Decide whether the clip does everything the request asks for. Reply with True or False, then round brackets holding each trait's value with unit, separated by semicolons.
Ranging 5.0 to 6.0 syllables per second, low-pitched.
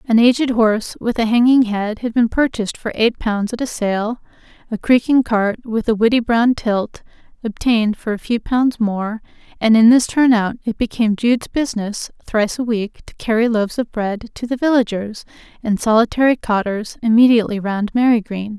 False (5.2 syllables/s; 225 Hz)